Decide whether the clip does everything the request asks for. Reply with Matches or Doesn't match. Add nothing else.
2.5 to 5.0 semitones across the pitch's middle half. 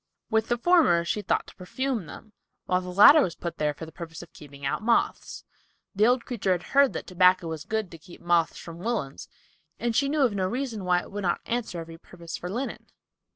Doesn't match